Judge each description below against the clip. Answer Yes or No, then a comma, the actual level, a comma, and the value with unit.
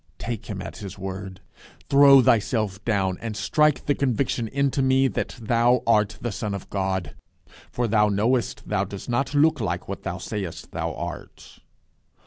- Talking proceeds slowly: No, average, 165 wpm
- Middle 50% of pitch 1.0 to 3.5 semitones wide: No, average, 4.6 semitones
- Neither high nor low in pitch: No, low, 110 Hz